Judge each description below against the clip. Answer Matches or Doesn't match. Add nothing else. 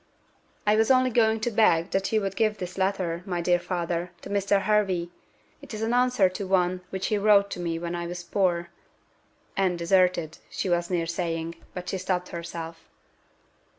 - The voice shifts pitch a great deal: Doesn't match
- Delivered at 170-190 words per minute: Matches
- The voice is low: Doesn't match